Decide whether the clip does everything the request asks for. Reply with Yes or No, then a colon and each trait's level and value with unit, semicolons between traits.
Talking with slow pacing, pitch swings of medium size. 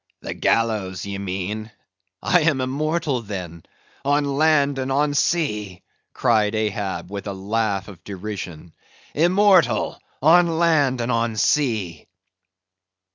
No: slow, 110 wpm; wide, 6.8 semitones